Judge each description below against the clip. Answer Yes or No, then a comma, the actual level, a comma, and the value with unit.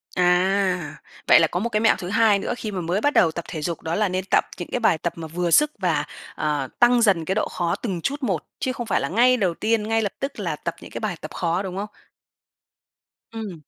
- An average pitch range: Yes, average, 4.6 semitones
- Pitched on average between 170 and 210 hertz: Yes, high, 190 Hz